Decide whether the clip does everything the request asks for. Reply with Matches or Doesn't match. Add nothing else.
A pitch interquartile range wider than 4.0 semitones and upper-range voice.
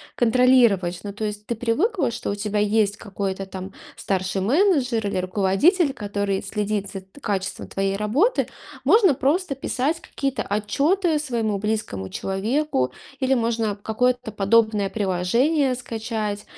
Matches